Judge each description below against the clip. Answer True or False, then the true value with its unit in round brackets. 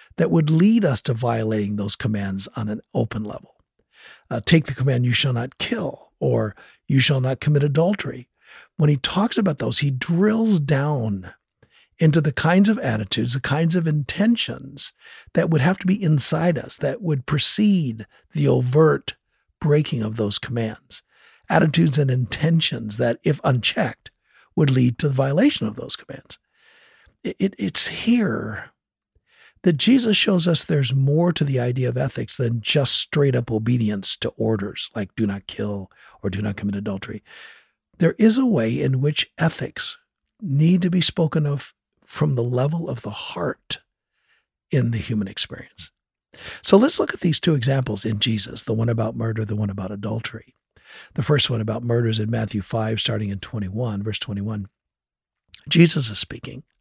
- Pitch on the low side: True (130 Hz)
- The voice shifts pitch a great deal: True (6.6 semitones)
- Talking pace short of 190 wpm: True (170 wpm)